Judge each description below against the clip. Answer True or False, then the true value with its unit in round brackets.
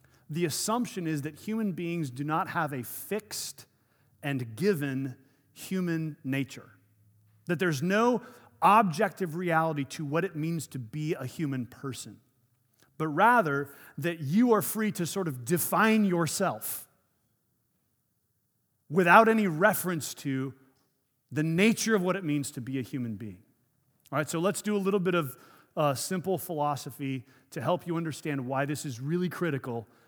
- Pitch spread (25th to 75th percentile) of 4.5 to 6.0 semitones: True (5.4 semitones)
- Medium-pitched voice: True (155 Hz)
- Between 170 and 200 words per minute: False (150 wpm)